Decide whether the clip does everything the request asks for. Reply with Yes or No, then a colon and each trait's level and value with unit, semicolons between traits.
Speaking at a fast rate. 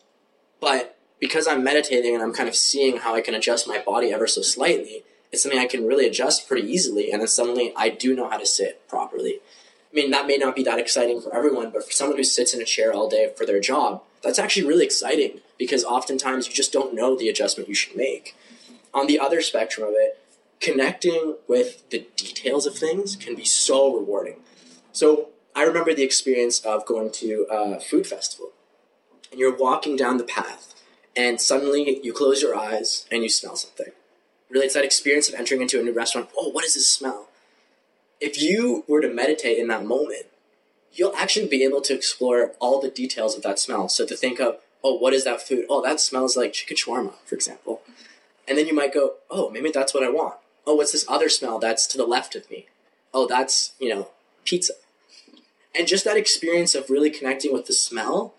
Yes: fast, 210 wpm